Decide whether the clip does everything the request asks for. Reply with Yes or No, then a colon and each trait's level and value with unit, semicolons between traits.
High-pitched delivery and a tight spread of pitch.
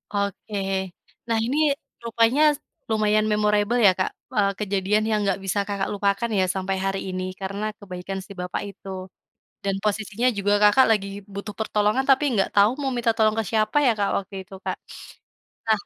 Yes: high, 205 Hz; narrow, 1.9 semitones